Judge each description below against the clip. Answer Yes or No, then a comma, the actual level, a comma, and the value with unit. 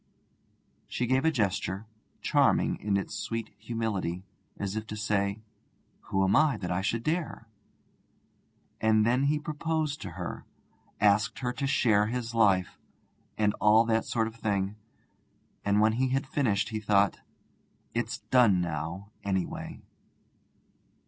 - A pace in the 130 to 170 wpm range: Yes, average, 140 wpm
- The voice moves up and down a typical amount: Yes, average, 3.6 semitones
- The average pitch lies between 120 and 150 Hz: No, low, 110 Hz